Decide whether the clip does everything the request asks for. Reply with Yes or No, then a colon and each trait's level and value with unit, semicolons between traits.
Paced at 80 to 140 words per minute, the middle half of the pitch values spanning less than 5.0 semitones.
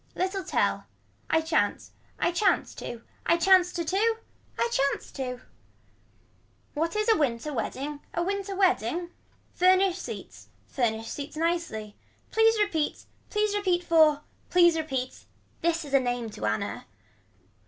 No: slow, 135 wpm; wide, 5.6 semitones